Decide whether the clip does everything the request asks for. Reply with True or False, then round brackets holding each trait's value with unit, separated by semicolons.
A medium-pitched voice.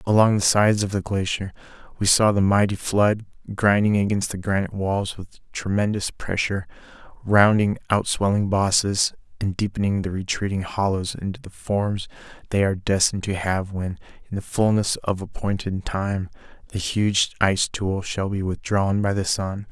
False (100 Hz)